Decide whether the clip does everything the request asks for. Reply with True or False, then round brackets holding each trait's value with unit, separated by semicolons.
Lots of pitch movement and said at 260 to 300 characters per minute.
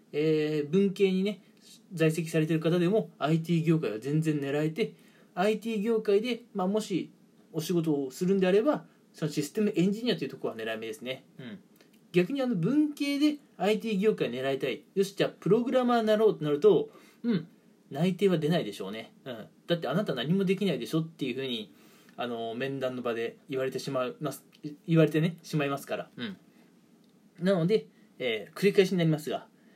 False (5.9 semitones; 345 characters per minute)